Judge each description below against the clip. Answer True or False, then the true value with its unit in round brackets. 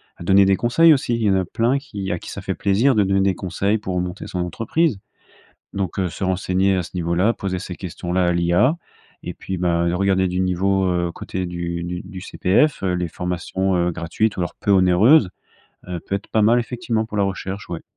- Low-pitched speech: True (95 Hz)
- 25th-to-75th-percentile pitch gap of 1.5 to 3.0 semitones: True (2.5 semitones)